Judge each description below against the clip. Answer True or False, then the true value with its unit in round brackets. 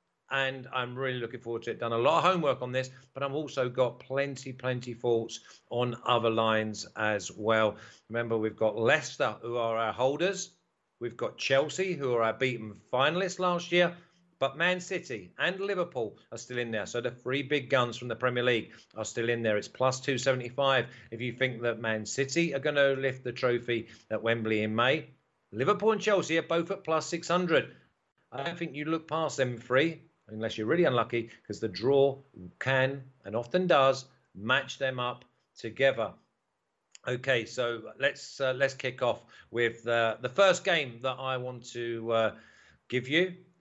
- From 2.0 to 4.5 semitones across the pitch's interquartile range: True (3.8 semitones)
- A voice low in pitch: True (130 Hz)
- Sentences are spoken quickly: False (185 wpm)